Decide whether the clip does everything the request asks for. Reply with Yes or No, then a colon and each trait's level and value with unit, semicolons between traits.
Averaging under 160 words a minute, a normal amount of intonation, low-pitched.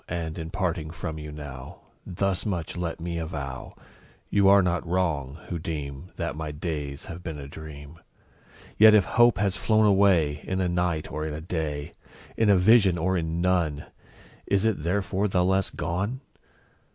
No: average, 175 wpm; average, 3.6 semitones; very low, 85 Hz